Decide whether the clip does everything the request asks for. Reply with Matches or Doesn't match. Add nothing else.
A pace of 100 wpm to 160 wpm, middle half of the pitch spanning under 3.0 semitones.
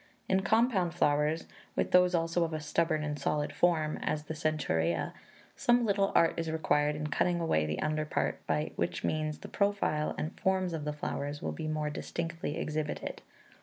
Doesn't match